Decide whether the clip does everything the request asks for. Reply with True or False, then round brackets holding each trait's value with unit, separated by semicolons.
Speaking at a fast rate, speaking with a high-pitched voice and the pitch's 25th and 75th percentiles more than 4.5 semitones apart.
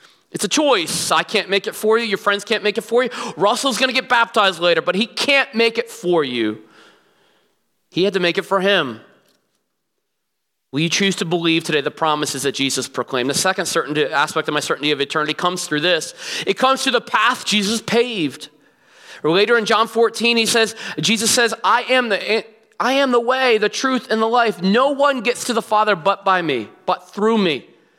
True (210 wpm; 210 Hz; 5.2 semitones)